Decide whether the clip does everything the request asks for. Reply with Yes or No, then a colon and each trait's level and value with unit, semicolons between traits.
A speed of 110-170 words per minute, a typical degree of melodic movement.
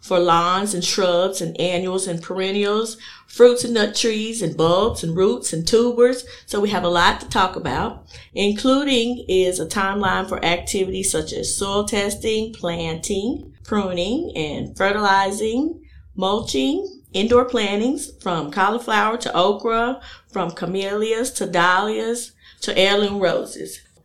Yes: slow, 135 wpm; average, 4.0 semitones